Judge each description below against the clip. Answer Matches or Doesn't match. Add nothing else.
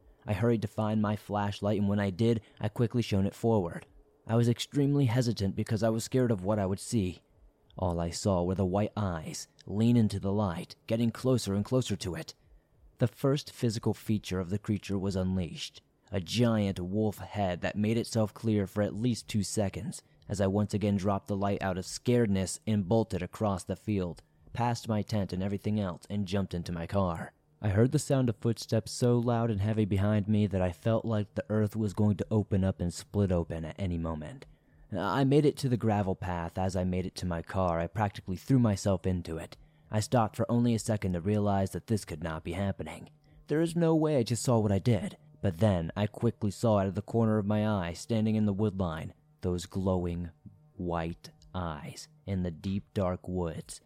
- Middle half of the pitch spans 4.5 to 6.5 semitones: Doesn't match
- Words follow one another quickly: Matches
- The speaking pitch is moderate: Doesn't match